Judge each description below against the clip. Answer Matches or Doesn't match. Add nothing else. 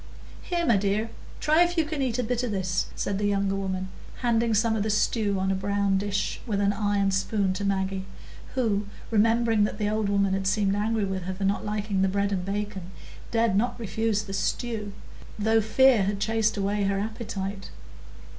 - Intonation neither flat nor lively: Doesn't match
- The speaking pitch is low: Doesn't match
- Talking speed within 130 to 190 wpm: Doesn't match